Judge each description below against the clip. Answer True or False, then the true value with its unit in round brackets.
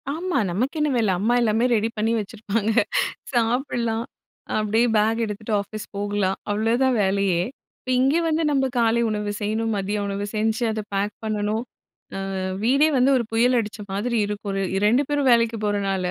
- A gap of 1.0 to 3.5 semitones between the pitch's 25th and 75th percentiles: True (2.6 semitones)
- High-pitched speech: True (220 Hz)